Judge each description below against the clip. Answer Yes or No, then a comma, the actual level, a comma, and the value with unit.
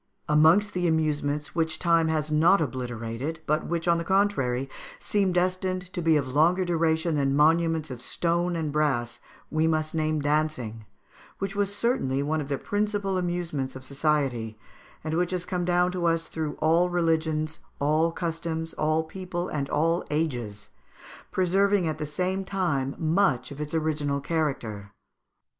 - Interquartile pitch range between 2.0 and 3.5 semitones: Yes, average, 3.1 semitones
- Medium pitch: Yes, medium, 160 Hz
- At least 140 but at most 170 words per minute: Yes, average, 155 wpm